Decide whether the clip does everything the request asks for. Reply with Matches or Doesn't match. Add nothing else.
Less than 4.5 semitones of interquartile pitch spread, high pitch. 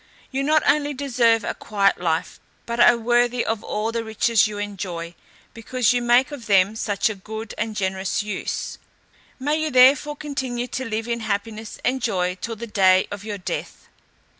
Matches